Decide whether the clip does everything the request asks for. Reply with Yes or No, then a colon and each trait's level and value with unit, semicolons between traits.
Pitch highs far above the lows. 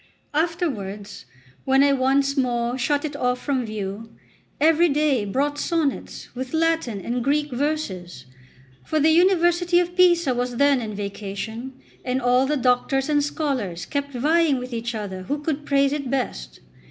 No: average, 4.2 semitones